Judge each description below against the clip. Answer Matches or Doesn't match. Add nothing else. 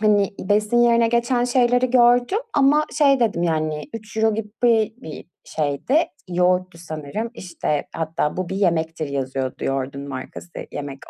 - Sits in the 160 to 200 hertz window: Matches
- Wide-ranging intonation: Matches